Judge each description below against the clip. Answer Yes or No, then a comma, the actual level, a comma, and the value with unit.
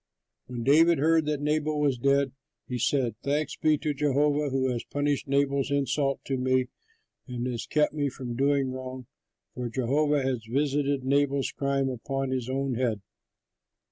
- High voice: No, low, 135 Hz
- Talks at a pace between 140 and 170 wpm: Yes, average, 160 wpm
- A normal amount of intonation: No, narrow, 2.0 semitones